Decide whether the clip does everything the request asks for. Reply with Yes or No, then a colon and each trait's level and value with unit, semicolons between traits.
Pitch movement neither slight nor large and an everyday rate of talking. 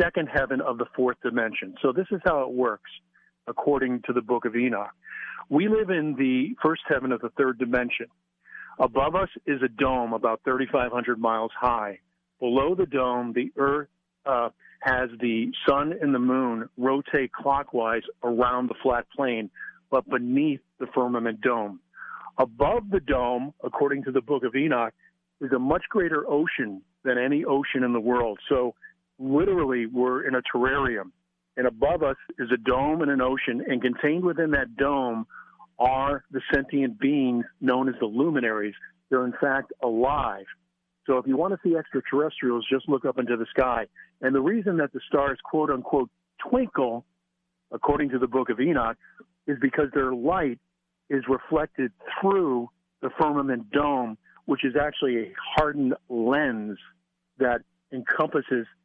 Yes: average, 3.8 semitones; average, 160 wpm